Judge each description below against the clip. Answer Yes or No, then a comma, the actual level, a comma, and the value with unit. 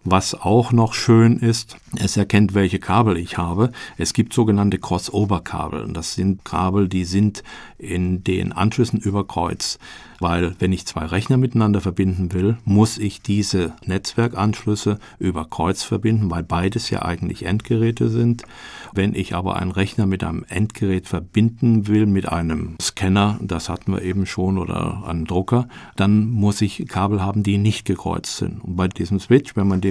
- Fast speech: No, average, 165 wpm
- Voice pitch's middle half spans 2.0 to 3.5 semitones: Yes, average, 2.9 semitones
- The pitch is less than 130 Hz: Yes, low, 100 Hz